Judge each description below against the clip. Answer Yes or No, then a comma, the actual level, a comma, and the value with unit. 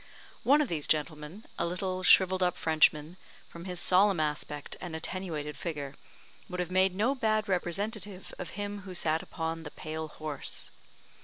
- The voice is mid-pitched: Yes, medium, 180 Hz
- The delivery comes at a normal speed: Yes, average, 160 wpm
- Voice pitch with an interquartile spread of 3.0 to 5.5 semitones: Yes, average, 3.5 semitones